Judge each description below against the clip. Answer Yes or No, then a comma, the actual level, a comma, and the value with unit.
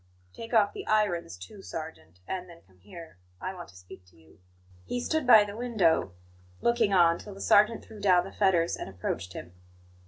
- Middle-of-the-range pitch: Yes, medium, 180 Hz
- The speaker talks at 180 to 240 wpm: Yes, average, 195 wpm